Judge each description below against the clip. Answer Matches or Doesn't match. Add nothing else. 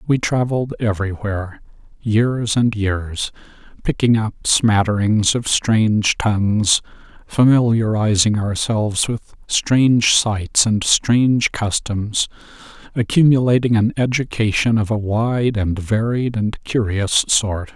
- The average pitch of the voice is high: Doesn't match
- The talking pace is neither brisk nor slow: Doesn't match